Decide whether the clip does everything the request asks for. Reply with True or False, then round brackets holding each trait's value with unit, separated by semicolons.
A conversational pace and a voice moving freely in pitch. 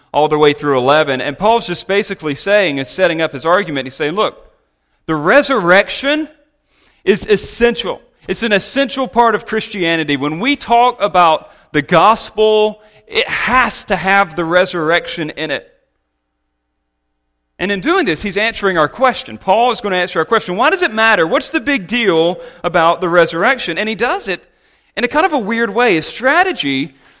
True (180 wpm; 6.9 semitones)